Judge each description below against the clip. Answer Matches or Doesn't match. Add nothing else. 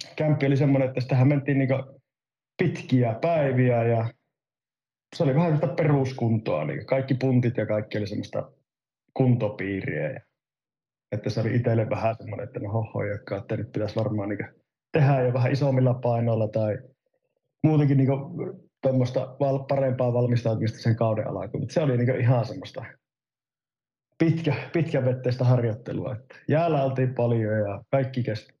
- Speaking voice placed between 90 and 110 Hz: Doesn't match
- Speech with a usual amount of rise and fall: Matches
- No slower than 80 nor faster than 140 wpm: Matches